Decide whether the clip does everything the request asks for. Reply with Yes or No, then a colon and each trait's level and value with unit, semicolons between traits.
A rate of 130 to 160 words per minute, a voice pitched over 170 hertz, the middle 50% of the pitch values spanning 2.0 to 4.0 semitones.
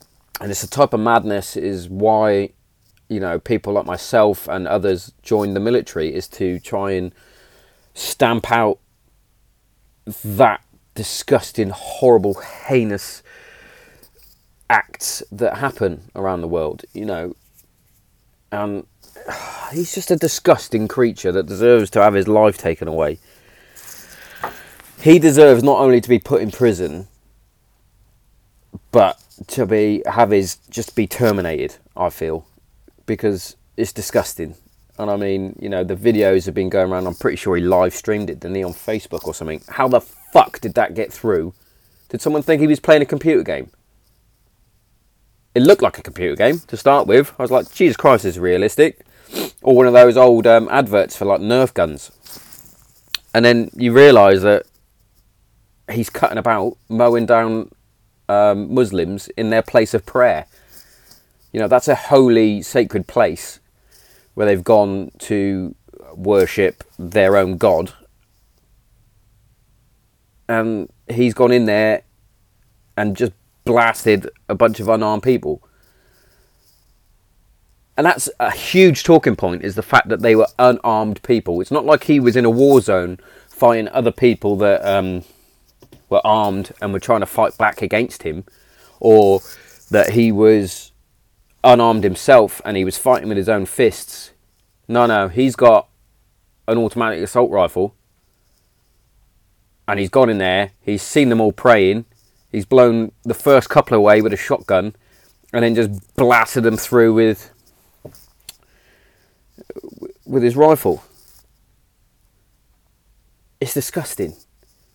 No: average, 145 wpm; low, 110 Hz; average, 3.3 semitones